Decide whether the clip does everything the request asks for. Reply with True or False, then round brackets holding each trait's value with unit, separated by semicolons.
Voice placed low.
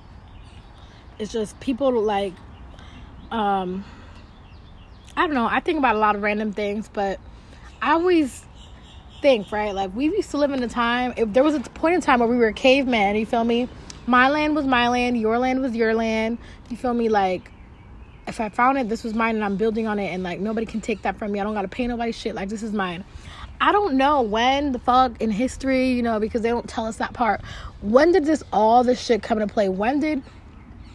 False (230 Hz)